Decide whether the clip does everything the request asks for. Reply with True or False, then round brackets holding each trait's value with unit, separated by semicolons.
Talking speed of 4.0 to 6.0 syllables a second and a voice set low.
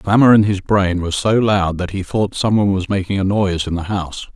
True (5.9 syllables/s; 95 Hz)